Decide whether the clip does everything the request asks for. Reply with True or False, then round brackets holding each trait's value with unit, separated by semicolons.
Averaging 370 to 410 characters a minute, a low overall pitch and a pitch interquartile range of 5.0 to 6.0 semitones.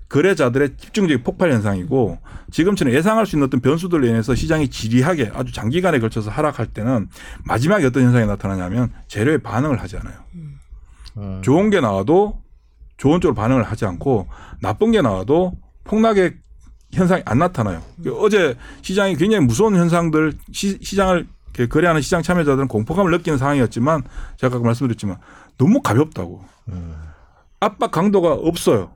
False (380 characters per minute; 130 Hz; 8.0 semitones)